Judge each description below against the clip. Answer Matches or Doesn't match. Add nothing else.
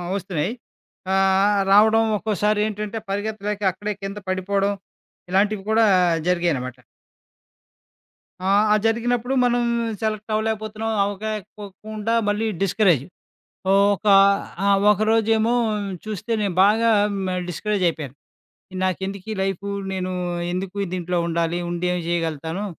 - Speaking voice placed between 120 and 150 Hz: Doesn't match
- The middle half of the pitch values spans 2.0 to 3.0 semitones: Matches